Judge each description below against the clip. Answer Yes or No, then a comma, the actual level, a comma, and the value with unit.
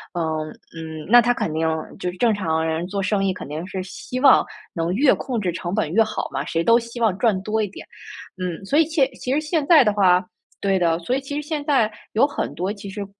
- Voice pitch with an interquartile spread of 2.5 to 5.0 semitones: No, wide, 5.6 semitones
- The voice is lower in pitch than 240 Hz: Yes, high, 205 Hz